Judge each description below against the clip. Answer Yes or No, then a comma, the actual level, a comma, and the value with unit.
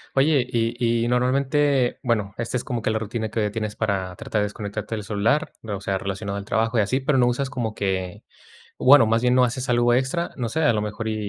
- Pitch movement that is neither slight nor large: Yes, average, 3.3 semitones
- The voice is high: No, low, 115 Hz